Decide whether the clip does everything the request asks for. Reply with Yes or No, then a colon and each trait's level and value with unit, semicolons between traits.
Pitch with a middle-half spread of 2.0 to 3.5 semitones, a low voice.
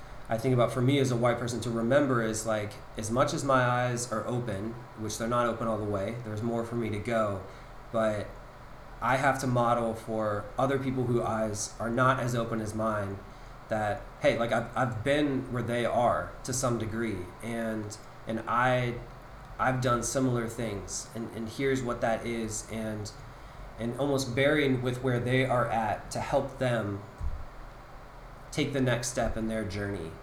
Yes: average, 2.7 semitones; low, 120 Hz